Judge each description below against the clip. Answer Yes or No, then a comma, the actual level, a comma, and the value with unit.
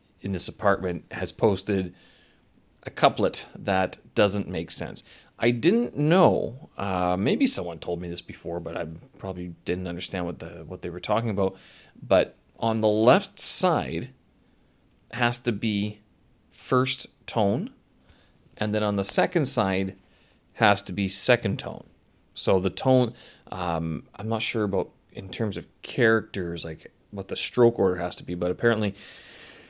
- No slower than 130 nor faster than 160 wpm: Yes, average, 155 wpm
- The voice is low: Yes, low, 100 Hz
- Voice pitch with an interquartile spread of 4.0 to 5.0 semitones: Yes, average, 4.3 semitones